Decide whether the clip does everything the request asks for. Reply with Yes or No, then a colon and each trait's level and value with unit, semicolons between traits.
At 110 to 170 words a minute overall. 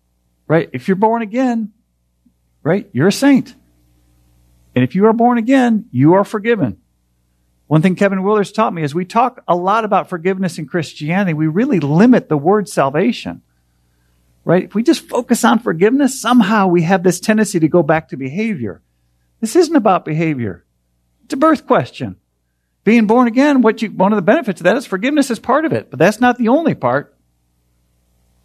No: average, 185 wpm